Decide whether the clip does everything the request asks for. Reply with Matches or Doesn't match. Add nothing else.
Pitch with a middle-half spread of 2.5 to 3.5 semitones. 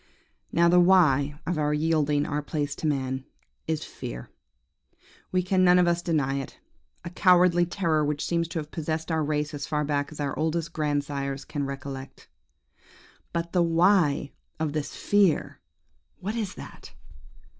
Matches